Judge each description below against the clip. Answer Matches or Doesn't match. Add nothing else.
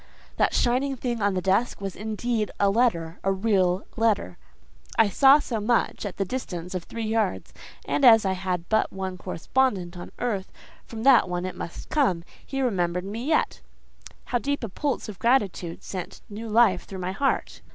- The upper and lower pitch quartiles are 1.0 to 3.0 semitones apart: Doesn't match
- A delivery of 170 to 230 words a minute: Matches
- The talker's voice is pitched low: Doesn't match